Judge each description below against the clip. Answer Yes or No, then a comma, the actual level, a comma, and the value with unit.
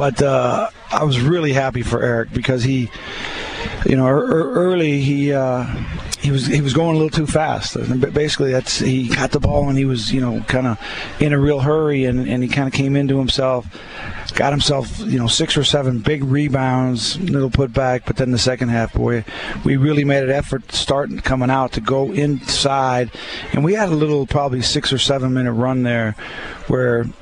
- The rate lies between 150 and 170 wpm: No, average, 200 wpm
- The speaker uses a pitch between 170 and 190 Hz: No, low, 135 Hz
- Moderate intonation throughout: No, narrow, 2.2 semitones